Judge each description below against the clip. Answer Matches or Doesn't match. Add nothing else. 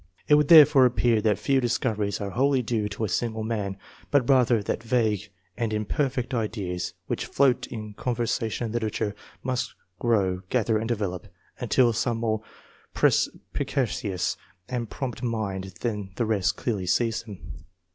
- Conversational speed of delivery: Matches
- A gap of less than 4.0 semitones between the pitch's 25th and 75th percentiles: Matches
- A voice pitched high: Doesn't match